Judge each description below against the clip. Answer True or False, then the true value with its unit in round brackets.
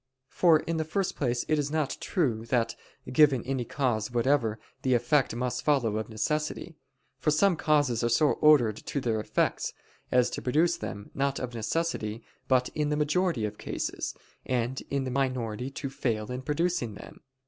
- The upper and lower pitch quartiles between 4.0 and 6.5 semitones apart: True (4.4 semitones)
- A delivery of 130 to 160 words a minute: False (175 wpm)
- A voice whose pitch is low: True (130 Hz)